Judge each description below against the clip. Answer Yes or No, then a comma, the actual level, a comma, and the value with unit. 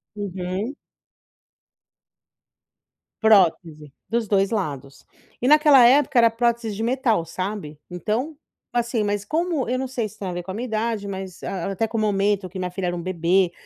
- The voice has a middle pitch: No, high, 205 Hz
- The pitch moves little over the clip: No, average, 4.4 semitones